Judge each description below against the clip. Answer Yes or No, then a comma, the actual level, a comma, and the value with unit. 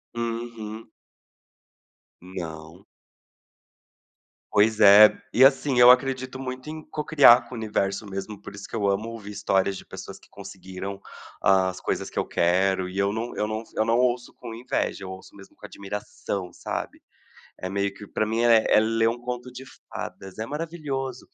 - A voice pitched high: No, low, 110 Hz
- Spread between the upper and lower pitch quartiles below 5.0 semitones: Yes, average, 3.8 semitones